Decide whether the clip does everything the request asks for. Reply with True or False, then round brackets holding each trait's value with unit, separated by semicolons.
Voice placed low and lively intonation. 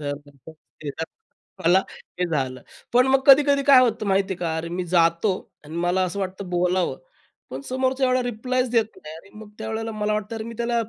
False (200 Hz; 5.7 semitones)